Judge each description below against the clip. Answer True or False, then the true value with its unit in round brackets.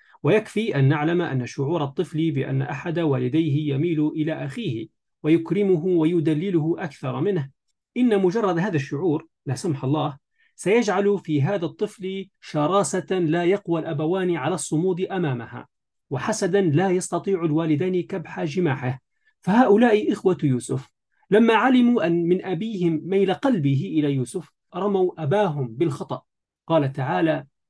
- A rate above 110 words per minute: True (125 wpm)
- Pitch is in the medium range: True (170 Hz)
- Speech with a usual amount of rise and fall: True (4.4 semitones)